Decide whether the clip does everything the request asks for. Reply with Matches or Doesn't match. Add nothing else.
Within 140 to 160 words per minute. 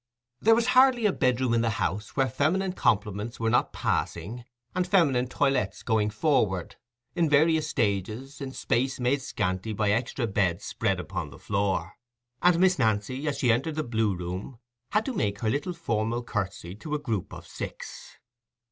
Doesn't match